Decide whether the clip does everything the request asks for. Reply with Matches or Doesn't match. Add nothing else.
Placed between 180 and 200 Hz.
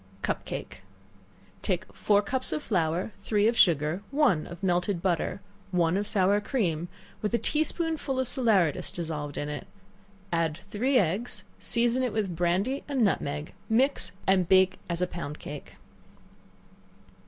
Matches